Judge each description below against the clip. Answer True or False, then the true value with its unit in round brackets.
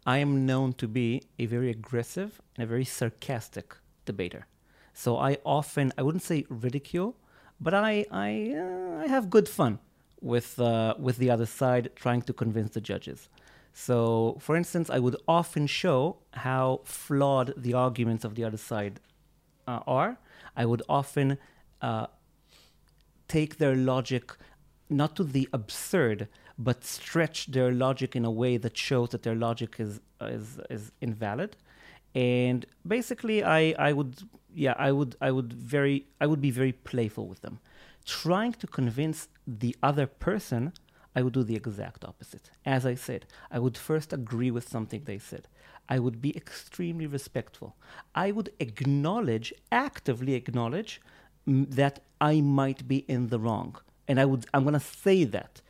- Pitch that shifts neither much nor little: True (3.8 semitones)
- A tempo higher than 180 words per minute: False (160 wpm)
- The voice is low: True (130 Hz)